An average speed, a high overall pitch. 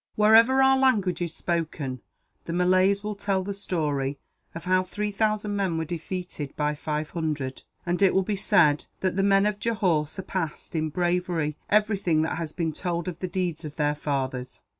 No: average, 180 wpm; medium, 180 Hz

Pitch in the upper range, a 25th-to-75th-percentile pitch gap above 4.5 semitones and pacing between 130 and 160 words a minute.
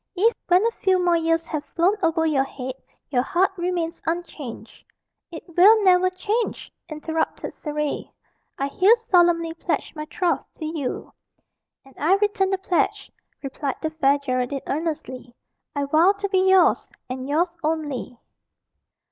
No: very high, 330 Hz; average, 4.2 semitones; average, 145 wpm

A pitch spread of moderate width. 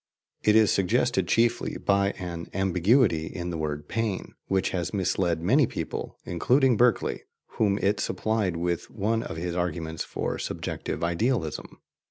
Yes: average, 4.3 semitones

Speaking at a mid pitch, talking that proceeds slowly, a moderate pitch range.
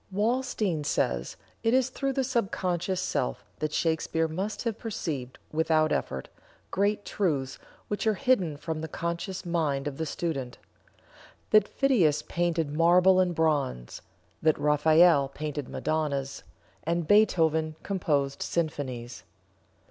Yes: medium, 160 Hz; slow, 125 wpm; average, 4.5 semitones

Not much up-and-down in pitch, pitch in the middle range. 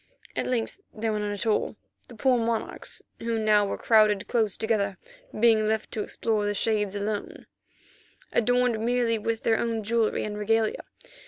No: narrow, 1.6 semitones; high, 220 Hz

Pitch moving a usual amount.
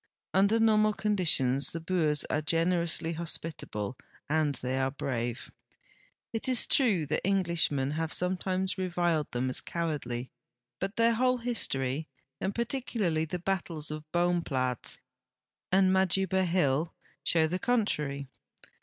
Yes: average, 4.5 semitones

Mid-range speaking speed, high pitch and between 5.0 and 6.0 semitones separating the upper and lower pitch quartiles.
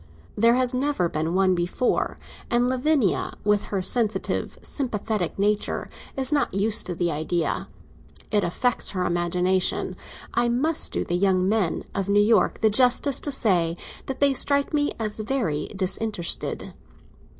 Yes: average, 150 wpm; high, 210 Hz; wide, 5.5 semitones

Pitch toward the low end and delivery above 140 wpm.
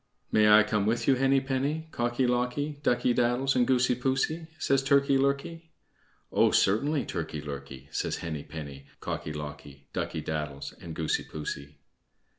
Yes: low, 120 Hz; average, 150 wpm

